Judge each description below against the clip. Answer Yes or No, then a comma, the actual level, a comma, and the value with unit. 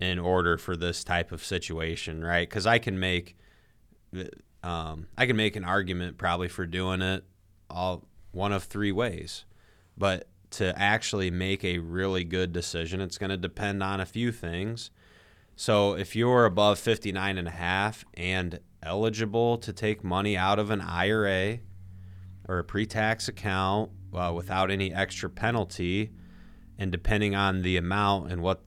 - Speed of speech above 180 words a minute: No, average, 155 wpm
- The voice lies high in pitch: No, very low, 95 Hz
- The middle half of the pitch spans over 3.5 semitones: No, narrow, 2.5 semitones